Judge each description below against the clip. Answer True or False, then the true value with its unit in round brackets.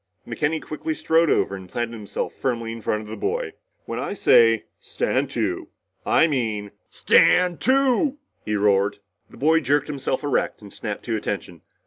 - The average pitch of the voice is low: True (125 Hz)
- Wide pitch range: True (7.3 semitones)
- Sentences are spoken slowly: False (165 wpm)